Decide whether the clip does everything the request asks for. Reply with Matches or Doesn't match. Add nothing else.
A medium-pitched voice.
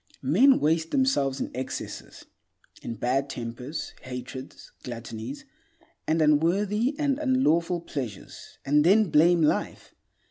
Matches